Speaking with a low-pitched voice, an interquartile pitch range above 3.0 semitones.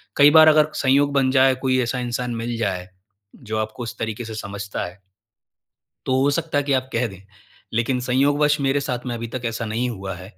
Yes: low, 125 Hz; average, 3.4 semitones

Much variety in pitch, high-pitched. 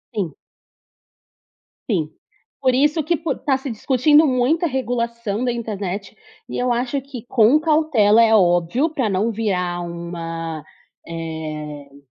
Yes: wide, 7.2 semitones; high, 225 Hz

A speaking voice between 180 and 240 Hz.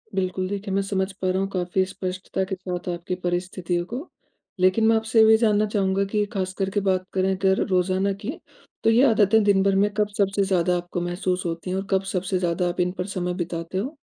Yes: high, 190 Hz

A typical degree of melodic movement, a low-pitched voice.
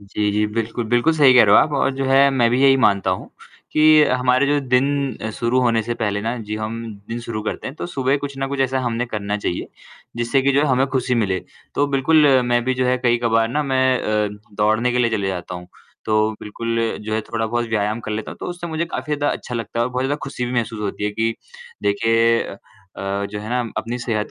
Yes: average, 3.5 semitones; low, 120 Hz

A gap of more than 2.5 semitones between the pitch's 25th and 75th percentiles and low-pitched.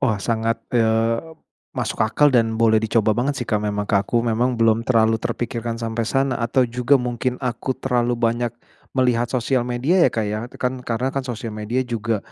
No: narrow, 2.0 semitones; low, 115 Hz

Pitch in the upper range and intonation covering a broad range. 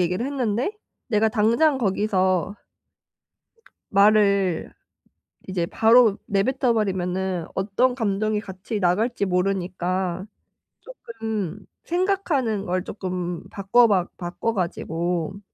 No: high, 200 Hz; average, 3.6 semitones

